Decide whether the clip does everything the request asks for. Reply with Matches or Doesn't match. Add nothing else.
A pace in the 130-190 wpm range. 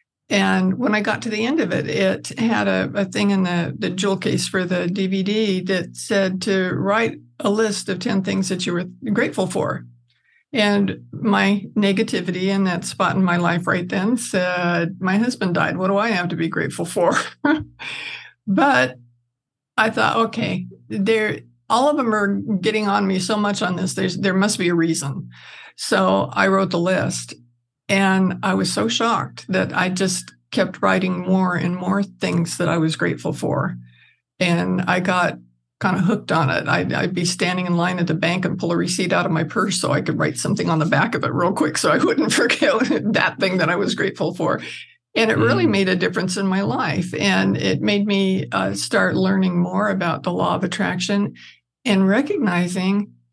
Doesn't match